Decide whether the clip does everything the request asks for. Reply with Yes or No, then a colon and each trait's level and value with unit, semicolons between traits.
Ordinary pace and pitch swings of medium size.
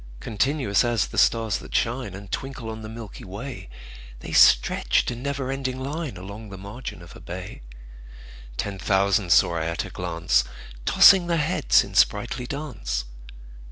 No: average, 160 wpm; wide, 5.8 semitones